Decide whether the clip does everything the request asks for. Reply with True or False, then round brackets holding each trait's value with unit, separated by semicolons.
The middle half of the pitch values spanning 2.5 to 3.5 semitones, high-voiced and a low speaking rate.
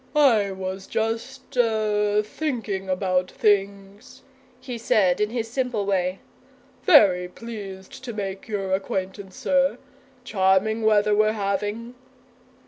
True (3.0 semitones; 210 Hz; 115 wpm)